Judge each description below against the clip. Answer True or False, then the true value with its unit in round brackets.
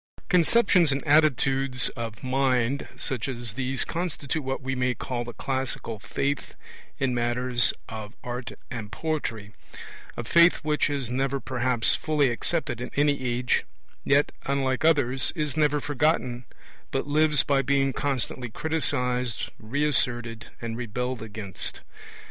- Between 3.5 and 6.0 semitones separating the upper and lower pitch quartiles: False (3.1 semitones)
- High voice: False (130 Hz)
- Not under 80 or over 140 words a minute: True (135 wpm)